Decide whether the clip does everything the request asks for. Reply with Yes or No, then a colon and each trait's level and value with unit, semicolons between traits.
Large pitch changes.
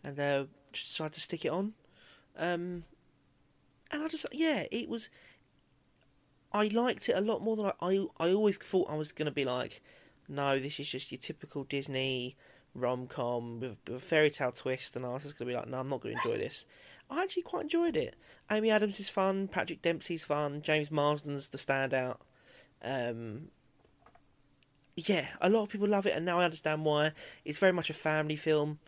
Yes: wide, 5.7 semitones